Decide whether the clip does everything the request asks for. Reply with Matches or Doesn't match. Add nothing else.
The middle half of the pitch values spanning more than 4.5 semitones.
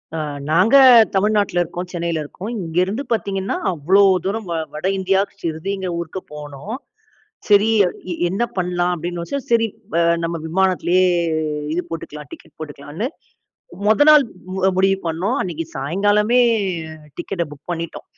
Doesn't match